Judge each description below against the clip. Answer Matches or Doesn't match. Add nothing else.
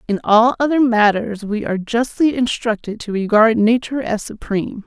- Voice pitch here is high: Matches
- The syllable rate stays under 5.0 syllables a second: Doesn't match